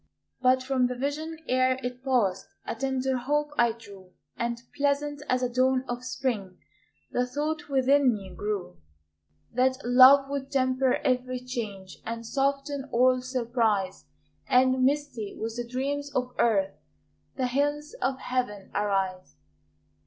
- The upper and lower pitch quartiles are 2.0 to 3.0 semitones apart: Yes, average, 2.7 semitones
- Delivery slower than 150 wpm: Yes, average, 140 wpm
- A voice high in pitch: Yes, very high, 255 Hz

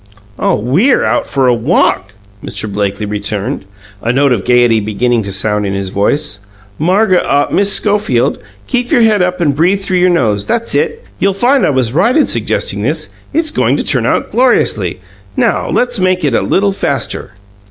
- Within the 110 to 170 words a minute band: No, average, 185 wpm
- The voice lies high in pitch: No, medium, 145 Hz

